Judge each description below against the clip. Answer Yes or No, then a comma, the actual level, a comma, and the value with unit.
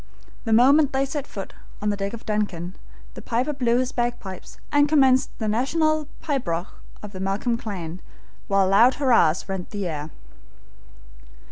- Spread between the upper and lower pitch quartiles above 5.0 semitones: Yes, wide, 5.5 semitones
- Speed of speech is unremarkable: Yes, average, 160 wpm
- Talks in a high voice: Yes, high, 225 Hz